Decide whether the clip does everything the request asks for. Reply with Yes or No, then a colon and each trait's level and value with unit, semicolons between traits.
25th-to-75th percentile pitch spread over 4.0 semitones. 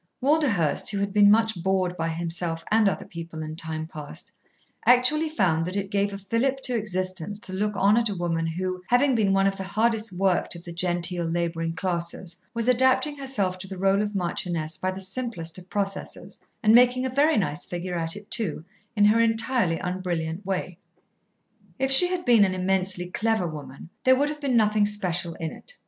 Yes: average, 4.6 semitones